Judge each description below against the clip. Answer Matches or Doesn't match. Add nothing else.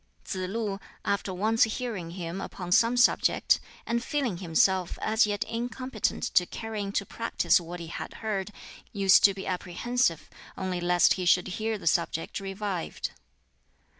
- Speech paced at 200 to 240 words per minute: Doesn't match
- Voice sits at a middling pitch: Doesn't match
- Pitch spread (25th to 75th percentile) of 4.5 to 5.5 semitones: Doesn't match